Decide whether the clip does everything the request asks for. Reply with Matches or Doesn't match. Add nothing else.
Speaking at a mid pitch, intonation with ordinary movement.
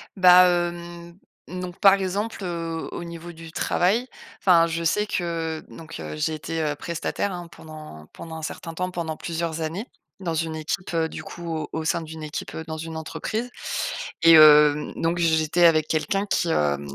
Doesn't match